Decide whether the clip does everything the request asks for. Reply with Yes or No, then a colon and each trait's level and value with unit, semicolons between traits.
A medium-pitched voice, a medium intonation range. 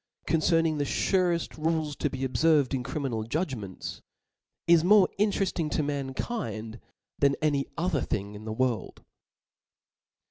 Yes: medium, 145 Hz; average, 4.4 semitones